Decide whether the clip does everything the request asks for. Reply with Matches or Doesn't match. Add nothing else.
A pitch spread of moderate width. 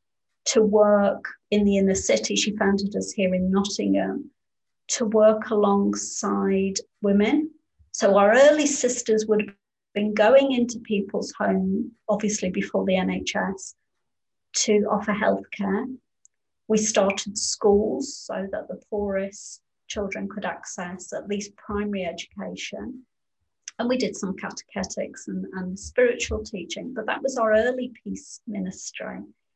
Doesn't match